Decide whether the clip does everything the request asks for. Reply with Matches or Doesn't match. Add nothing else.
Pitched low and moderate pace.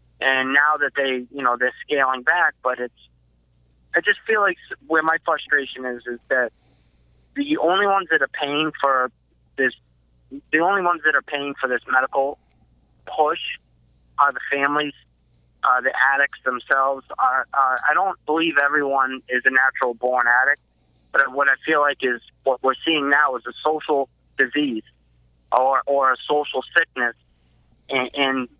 Matches